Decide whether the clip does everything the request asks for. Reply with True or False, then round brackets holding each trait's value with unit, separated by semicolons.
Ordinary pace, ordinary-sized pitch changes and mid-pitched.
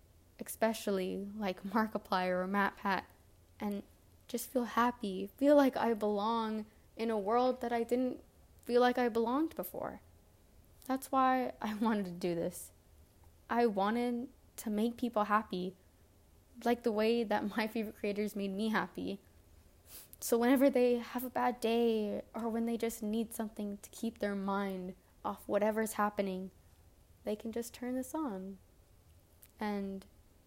False (145 wpm; 3.9 semitones; 210 Hz)